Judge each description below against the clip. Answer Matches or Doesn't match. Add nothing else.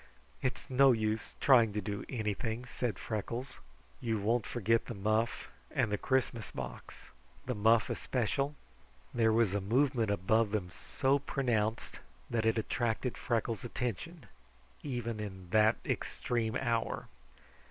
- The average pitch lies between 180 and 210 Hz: Doesn't match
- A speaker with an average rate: Doesn't match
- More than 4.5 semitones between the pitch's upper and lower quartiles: Doesn't match